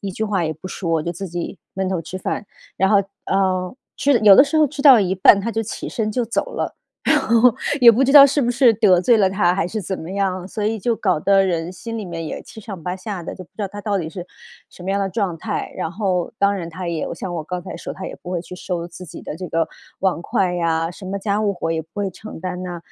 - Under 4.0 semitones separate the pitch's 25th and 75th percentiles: Yes, average, 3.3 semitones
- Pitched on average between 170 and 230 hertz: Yes, high, 190 Hz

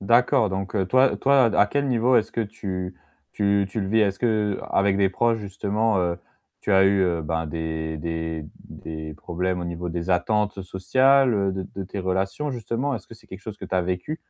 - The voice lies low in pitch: Yes, very low, 95 Hz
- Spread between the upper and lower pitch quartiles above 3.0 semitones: Yes, average, 3.7 semitones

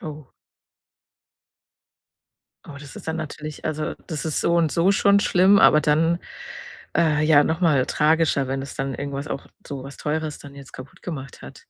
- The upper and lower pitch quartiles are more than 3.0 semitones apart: No, narrow, 2.6 semitones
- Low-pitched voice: No, medium, 150 Hz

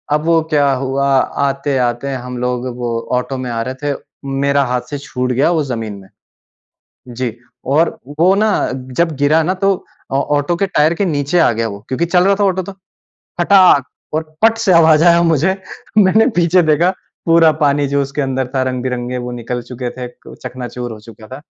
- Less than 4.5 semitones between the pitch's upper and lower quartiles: No, average, 5.0 semitones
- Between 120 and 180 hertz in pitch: Yes, medium, 140 Hz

